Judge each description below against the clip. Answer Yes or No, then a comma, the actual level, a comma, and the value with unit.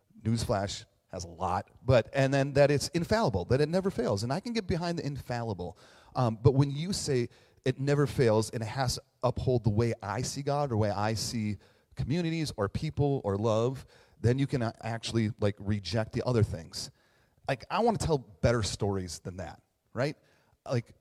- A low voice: Yes, low, 120 Hz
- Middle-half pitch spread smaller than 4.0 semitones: No, average, 4.5 semitones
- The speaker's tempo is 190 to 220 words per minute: Yes, average, 195 wpm